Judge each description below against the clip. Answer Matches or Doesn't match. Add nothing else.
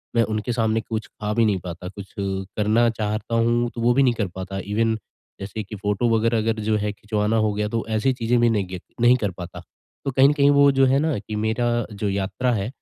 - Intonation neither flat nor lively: Doesn't match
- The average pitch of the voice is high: Doesn't match